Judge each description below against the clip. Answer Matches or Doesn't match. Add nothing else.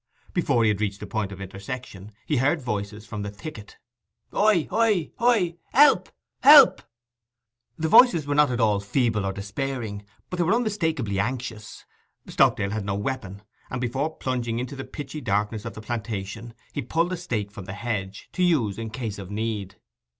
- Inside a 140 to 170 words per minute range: Doesn't match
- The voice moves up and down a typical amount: Doesn't match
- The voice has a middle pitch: Doesn't match